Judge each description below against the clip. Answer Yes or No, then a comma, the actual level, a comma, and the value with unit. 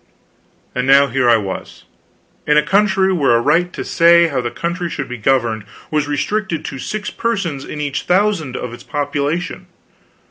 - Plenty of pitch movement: No, average, 4.9 semitones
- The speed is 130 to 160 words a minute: No, average, 175 wpm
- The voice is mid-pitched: Yes, medium, 150 Hz